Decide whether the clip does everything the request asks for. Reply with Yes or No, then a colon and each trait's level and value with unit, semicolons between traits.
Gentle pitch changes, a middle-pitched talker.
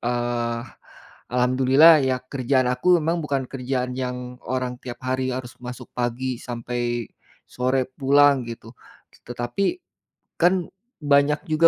No: narrow, 2.3 semitones; low, 130 Hz